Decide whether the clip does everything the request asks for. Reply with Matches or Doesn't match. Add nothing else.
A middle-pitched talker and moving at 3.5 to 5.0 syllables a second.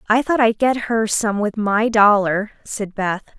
Doesn't match